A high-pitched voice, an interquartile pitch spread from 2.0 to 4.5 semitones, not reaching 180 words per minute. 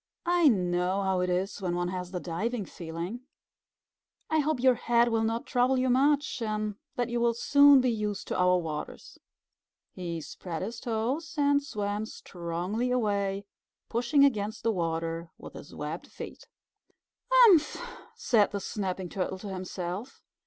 No: high, 215 Hz; wide, 5.4 semitones; average, 155 wpm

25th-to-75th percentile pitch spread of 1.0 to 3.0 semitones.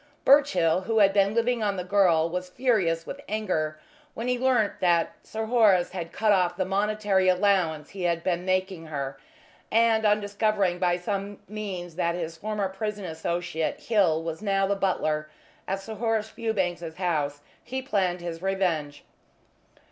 No: average, 3.6 semitones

